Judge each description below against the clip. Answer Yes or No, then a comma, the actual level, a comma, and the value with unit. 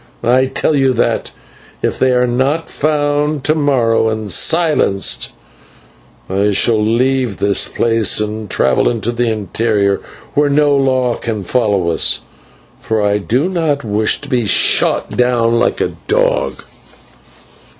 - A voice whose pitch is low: Yes, low, 120 Hz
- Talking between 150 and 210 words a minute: No, average, 140 wpm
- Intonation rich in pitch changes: No, average, 4.7 semitones